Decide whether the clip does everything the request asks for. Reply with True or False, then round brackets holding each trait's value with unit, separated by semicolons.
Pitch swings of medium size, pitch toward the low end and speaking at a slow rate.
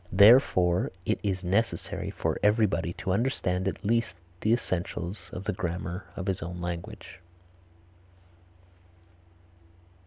True (3.4 semitones; 95 Hz; 115 wpm)